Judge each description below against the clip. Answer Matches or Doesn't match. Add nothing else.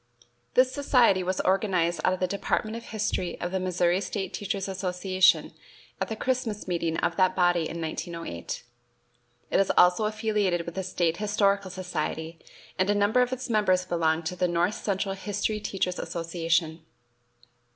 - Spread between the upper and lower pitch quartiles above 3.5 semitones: Doesn't match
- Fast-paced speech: Doesn't match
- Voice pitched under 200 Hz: Matches